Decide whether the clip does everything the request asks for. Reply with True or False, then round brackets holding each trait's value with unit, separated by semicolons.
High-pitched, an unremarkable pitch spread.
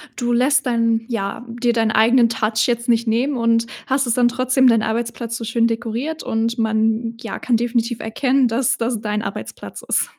False (235 Hz; 1.5 semitones)